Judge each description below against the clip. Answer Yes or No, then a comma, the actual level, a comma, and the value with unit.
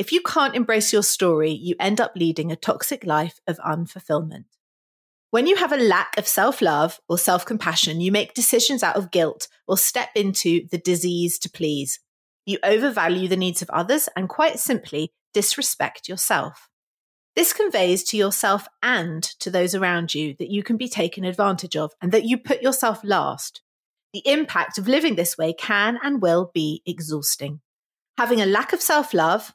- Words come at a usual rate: Yes, average, 180 wpm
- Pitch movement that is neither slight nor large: No, wide, 5.8 semitones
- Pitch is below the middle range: No, high, 195 Hz